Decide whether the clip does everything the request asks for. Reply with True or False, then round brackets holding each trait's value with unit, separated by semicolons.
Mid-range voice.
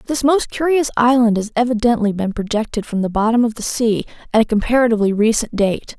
False (230 Hz)